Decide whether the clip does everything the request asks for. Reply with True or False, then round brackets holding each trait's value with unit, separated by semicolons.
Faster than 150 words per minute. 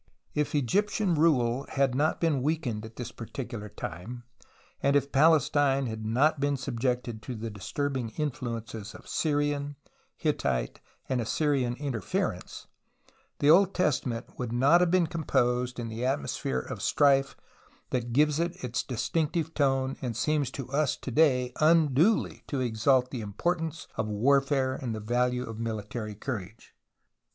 False (145 wpm)